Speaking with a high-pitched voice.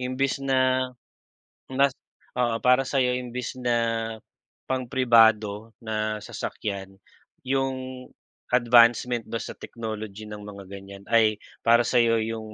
No: low, 115 Hz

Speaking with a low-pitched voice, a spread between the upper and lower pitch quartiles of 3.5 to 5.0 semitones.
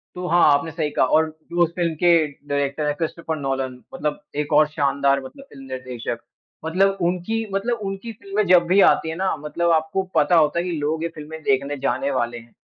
No: medium, 160 Hz; average, 3.8 semitones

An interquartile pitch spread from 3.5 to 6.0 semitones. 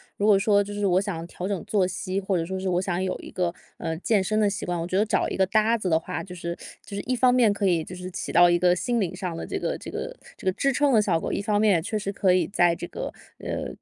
No: average, 2.9 semitones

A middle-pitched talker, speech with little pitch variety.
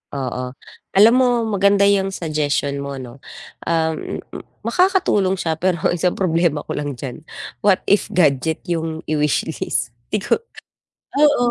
No: medium, 165 Hz; wide, 5.4 semitones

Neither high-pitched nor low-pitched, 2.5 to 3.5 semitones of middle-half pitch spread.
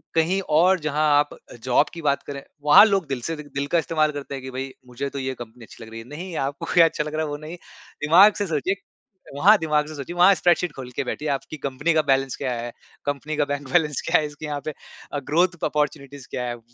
Yes: medium, 150 Hz; average, 2.9 semitones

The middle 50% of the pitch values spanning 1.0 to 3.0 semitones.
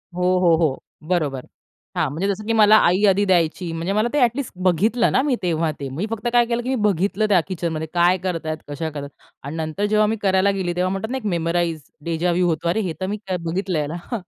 No: average, 4.5 semitones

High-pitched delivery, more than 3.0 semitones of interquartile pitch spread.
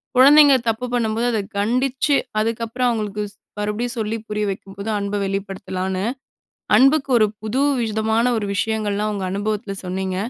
No: high, 215 Hz; average, 2.7 semitones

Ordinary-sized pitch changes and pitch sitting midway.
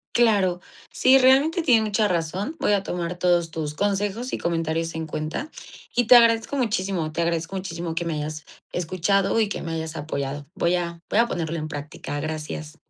Yes: average, 4.5 semitones; medium, 175 Hz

